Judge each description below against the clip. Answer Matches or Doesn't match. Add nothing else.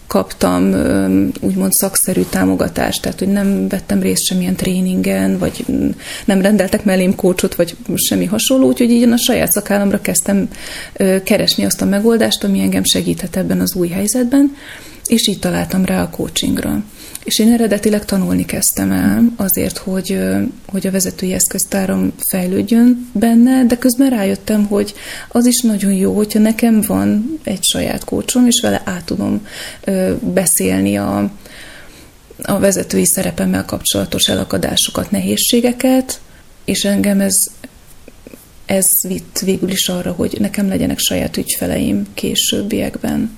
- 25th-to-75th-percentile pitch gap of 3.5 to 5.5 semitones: Matches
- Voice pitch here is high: Matches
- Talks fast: Doesn't match